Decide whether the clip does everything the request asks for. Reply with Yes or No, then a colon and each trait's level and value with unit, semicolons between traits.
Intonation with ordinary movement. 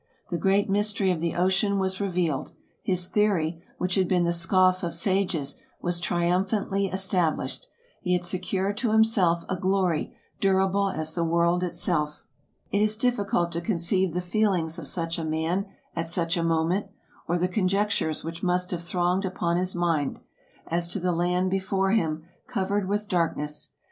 No: narrow, 2.3 semitones